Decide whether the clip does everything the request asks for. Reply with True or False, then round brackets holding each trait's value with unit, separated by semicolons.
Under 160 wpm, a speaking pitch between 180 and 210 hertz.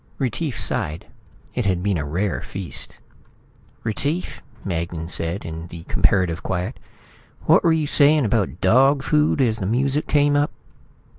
False (145 wpm; 105 Hz)